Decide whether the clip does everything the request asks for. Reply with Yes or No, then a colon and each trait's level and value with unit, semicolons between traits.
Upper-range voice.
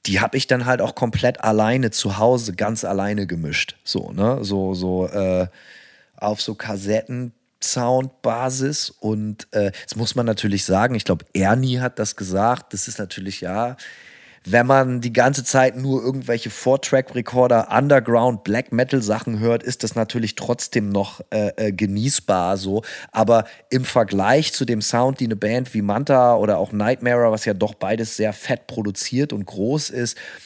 No: low, 115 Hz